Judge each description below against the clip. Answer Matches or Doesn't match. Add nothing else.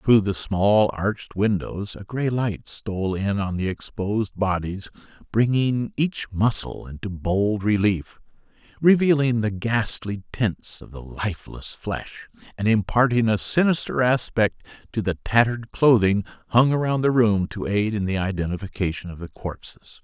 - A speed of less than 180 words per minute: Matches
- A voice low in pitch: Matches